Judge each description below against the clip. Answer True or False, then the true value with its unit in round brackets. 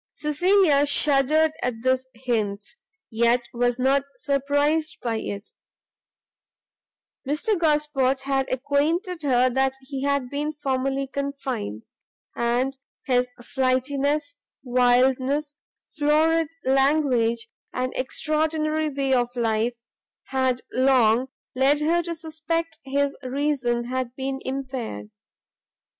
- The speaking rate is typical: False (100 wpm)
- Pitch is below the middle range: False (270 Hz)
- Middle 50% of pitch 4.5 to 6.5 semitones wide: False (2.9 semitones)